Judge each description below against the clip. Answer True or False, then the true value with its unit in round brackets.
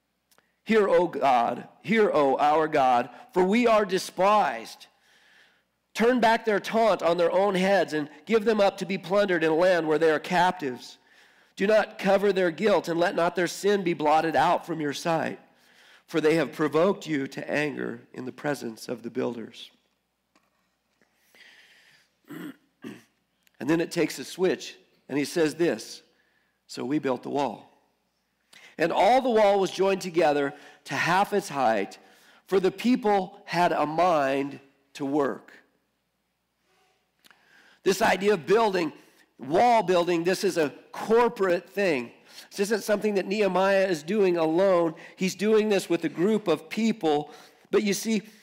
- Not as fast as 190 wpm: True (155 wpm)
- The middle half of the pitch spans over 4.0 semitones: True (4.5 semitones)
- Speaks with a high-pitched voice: False (180 Hz)